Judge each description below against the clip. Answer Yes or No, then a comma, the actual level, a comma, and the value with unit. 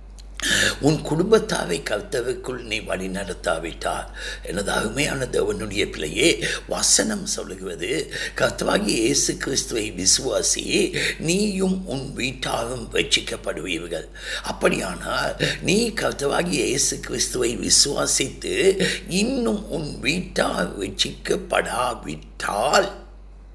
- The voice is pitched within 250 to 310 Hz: No, high, 200 Hz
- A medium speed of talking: No, slow, 70 wpm